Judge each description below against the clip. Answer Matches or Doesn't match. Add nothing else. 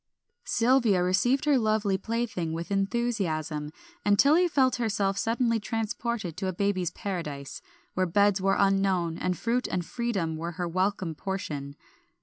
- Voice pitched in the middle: Doesn't match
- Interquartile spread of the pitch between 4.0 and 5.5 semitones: Matches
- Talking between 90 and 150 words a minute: Matches